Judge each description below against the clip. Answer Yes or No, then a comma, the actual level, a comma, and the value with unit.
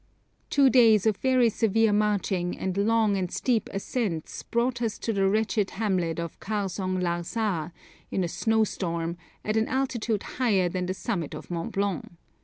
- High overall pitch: Yes, high, 205 Hz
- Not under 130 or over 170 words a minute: Yes, average, 165 wpm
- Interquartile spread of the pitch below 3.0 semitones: No, average, 3.7 semitones